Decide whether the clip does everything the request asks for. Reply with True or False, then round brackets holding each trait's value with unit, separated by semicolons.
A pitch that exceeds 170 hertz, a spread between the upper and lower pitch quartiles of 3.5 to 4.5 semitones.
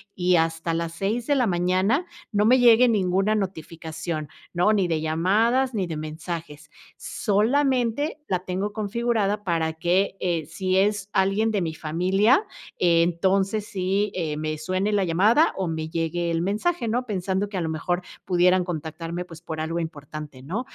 True (185 Hz; 4.1 semitones)